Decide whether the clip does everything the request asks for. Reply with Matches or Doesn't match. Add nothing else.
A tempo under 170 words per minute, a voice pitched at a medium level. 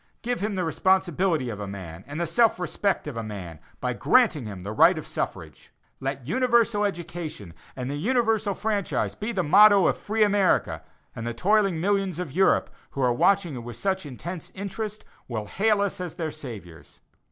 Doesn't match